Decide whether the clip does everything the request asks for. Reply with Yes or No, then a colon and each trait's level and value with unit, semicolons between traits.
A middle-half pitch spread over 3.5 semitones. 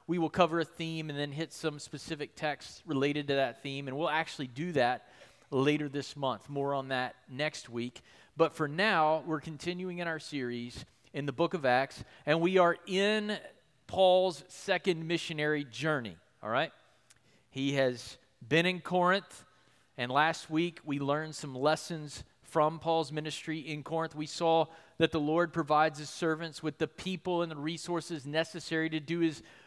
No: average, 3.0 semitones